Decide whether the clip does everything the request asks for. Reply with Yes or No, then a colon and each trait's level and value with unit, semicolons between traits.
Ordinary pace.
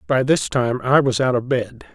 No: fast, 245 wpm